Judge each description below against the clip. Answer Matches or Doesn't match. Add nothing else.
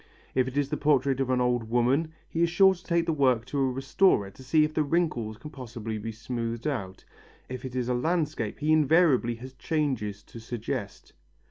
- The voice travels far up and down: Doesn't match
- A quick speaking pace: Matches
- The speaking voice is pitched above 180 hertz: Doesn't match